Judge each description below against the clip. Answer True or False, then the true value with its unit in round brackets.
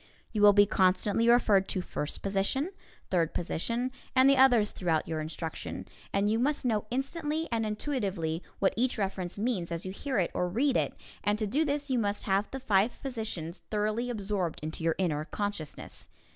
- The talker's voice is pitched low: False (205 Hz)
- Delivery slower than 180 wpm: False (185 wpm)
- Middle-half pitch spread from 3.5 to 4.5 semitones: False (5.2 semitones)